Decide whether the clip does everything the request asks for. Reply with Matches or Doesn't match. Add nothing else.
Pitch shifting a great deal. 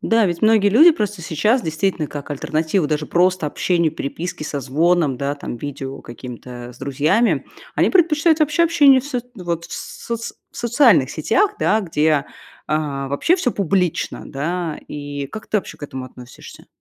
Matches